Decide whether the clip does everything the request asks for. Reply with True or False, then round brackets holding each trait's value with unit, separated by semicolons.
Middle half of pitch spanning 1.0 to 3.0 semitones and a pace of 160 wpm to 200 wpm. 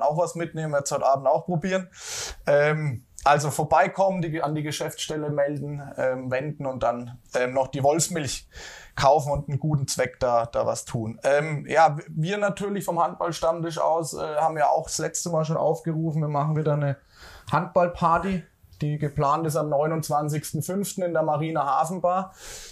True (2.7 semitones; 170 wpm)